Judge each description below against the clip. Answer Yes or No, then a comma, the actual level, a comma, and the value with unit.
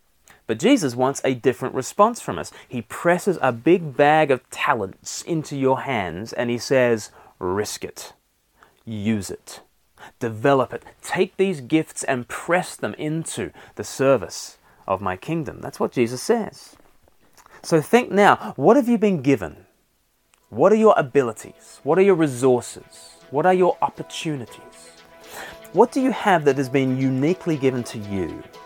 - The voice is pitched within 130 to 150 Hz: Yes, low, 135 Hz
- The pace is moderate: Yes, average, 155 wpm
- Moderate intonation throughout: No, wide, 6.1 semitones